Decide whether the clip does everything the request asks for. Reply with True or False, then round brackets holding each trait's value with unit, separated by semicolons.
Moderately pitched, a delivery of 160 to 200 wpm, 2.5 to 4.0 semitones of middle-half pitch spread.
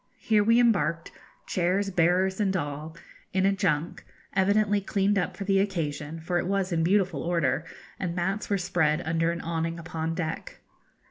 True (180 Hz; 165 wpm; 3.1 semitones)